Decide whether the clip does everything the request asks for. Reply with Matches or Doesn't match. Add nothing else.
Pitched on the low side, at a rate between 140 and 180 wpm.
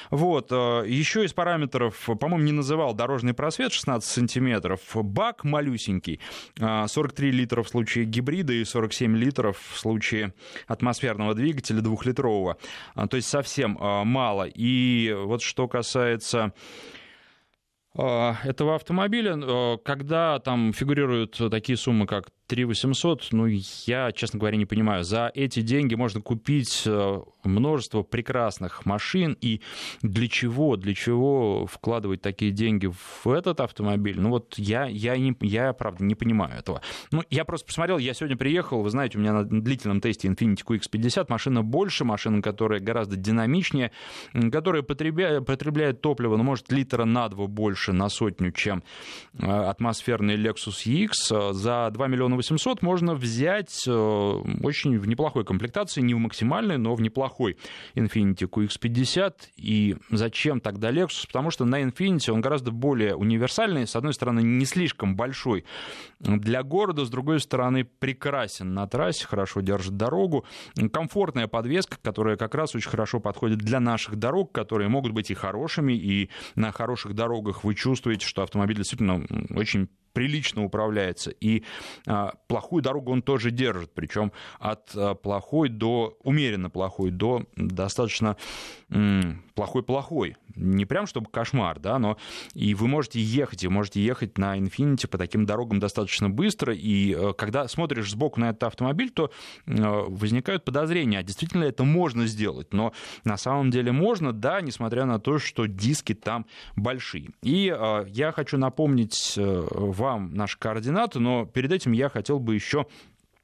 Matches